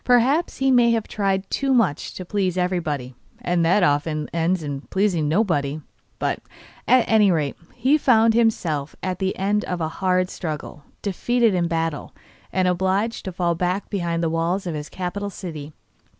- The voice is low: No, medium, 185 Hz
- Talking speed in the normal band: Yes, average, 170 wpm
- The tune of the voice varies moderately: Yes, average, 4.1 semitones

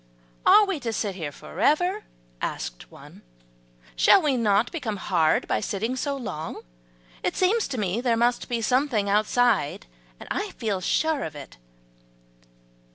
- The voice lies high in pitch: Yes, high, 230 Hz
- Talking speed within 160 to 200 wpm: No, average, 150 wpm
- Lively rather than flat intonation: Yes, wide, 6.0 semitones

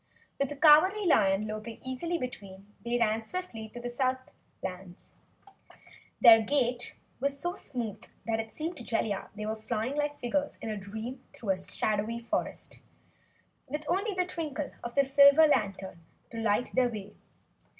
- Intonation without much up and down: No, average, 5.0 semitones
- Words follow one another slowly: No, average, 155 wpm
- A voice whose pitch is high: Yes, high, 240 Hz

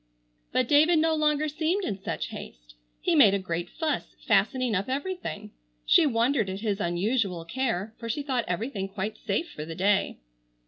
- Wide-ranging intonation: Yes, wide, 7.0 semitones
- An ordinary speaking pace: Yes, average, 175 wpm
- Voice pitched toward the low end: No, high, 225 Hz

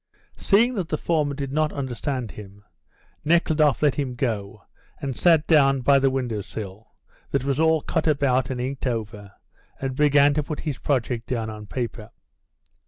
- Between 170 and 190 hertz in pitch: No, low, 135 Hz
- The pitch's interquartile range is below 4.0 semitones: No, average, 4.3 semitones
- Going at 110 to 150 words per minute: No, average, 170 wpm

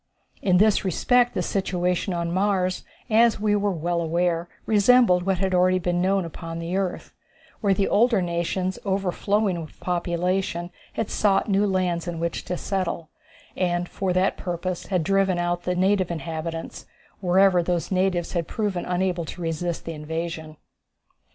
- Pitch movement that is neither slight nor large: No, narrow, 2.1 semitones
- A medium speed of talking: Yes, average, 155 wpm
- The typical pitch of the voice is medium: Yes, medium, 180 Hz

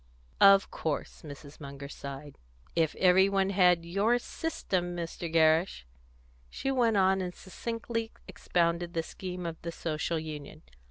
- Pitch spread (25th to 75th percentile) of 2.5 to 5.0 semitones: Yes, average, 3.4 semitones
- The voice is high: No, medium, 175 Hz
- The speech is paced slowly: Yes, slow, 130 wpm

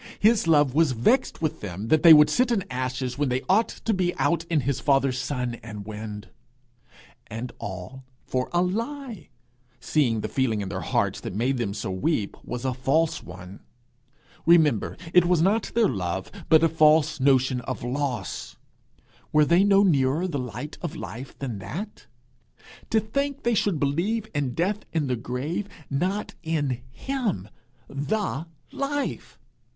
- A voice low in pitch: No, medium, 145 Hz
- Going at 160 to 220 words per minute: Yes, average, 165 wpm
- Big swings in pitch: Yes, wide, 6.4 semitones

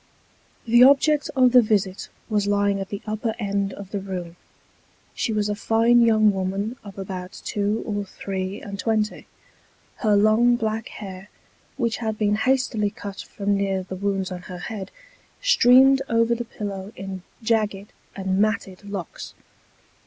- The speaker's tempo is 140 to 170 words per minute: Yes, average, 155 wpm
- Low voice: No, high, 205 Hz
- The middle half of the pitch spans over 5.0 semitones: No, narrow, 2.5 semitones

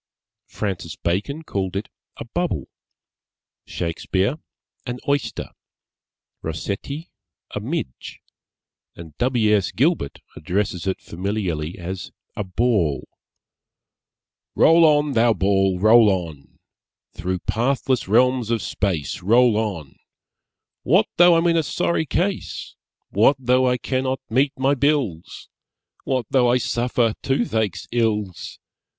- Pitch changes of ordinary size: No, wide, 5.8 semitones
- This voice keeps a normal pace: No, slow, 115 wpm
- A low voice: Yes, low, 110 Hz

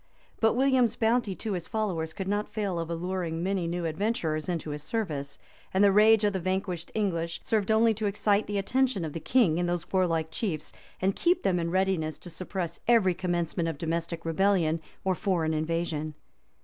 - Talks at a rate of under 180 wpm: No, average, 190 wpm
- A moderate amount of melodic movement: Yes, average, 3.9 semitones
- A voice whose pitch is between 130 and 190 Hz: Yes, medium, 185 Hz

